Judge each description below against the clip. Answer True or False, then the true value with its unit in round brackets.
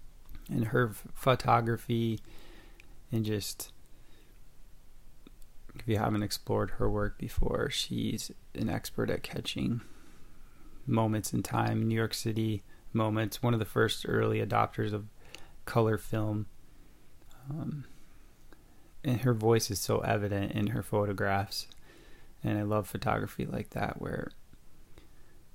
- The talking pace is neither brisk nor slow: False (115 wpm)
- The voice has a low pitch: True (110 Hz)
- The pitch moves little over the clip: True (1.8 semitones)